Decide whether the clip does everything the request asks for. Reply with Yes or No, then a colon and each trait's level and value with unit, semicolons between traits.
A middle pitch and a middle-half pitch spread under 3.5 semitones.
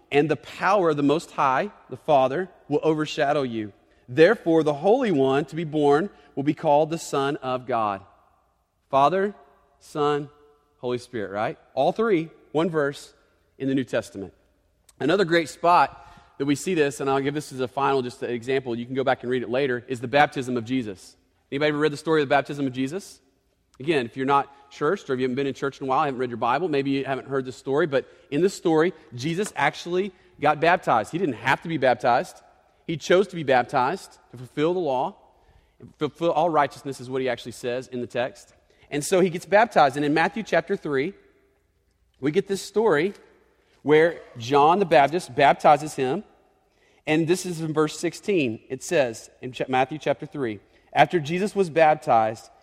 No: medium, 145 Hz; average, 4.0 semitones